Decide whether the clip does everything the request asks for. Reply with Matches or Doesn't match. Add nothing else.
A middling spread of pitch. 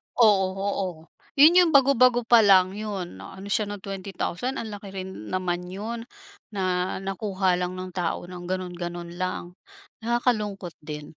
Matches